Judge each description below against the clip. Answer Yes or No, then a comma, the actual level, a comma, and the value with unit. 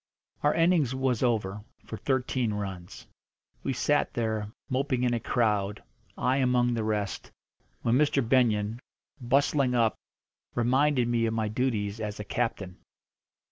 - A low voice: Yes, low, 120 Hz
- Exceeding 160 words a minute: No, average, 140 wpm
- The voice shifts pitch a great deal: No, average, 3.4 semitones